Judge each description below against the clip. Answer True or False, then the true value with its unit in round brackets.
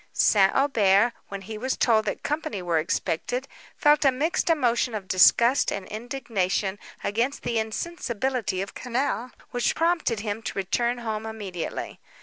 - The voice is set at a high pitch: True (230 Hz)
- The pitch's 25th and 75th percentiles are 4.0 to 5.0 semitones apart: True (4.5 semitones)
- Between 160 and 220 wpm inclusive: False (145 wpm)